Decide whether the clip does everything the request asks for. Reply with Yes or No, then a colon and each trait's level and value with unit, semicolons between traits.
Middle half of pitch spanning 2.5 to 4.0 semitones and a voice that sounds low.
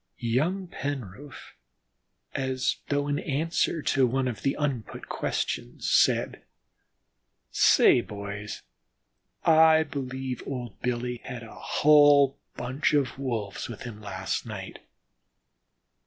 Yes: average, 3.3 semitones; low, 130 Hz